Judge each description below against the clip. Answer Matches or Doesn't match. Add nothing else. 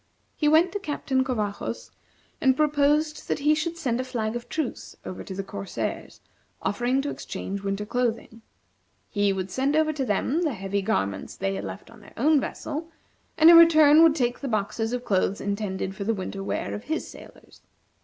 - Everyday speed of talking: Matches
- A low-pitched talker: Doesn't match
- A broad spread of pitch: Matches